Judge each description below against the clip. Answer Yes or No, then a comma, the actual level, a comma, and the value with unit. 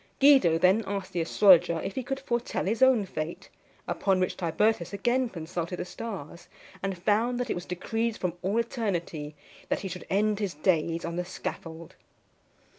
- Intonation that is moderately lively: Yes, average, 4.8 semitones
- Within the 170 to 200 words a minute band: Yes, average, 175 wpm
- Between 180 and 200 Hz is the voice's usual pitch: Yes, high, 190 Hz